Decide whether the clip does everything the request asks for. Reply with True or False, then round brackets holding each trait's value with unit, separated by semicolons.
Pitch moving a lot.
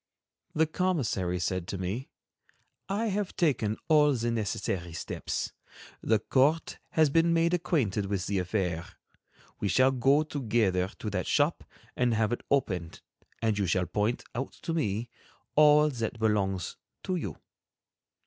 True (7.7 semitones)